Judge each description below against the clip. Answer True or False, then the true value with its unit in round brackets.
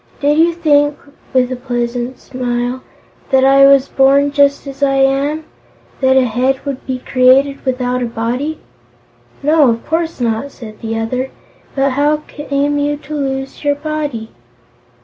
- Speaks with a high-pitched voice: True (270 Hz)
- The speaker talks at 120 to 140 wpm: False (155 wpm)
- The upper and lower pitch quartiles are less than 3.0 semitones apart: True (2.4 semitones)